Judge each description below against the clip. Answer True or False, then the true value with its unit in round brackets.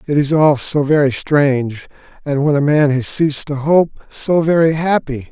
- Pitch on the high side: False (145 Hz)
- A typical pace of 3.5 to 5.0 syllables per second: True (4.6 syllables/s)